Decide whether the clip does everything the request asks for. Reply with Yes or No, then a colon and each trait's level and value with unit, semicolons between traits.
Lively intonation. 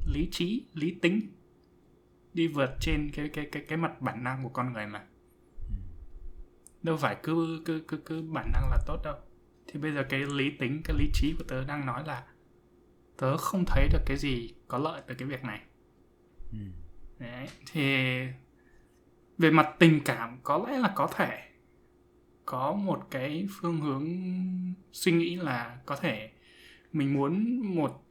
Yes: wide, 6.0 semitones